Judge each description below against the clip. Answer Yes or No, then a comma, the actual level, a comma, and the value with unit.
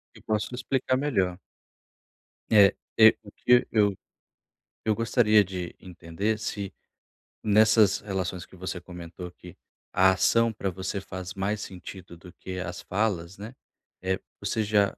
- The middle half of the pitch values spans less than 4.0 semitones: Yes, average, 2.8 semitones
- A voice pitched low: Yes, low, 100 Hz